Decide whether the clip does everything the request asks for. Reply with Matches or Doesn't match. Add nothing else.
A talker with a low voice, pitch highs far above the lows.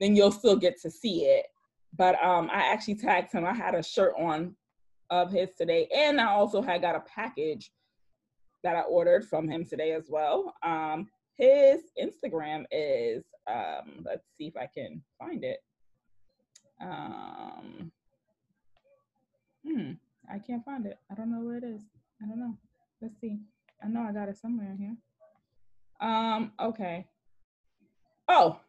Doesn't match